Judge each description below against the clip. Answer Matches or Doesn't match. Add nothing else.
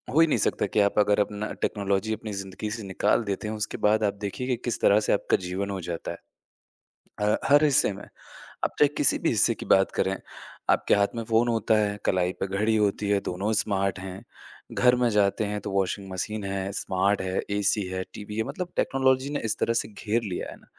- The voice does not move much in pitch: Matches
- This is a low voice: Matches